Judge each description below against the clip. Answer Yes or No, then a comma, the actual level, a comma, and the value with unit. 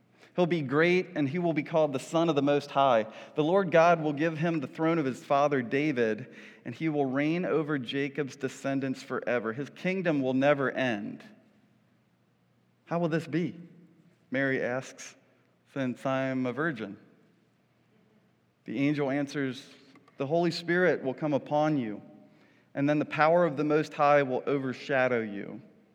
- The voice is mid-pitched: Yes, medium, 145 Hz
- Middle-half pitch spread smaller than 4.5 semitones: Yes, average, 3.4 semitones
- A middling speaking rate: Yes, average, 160 wpm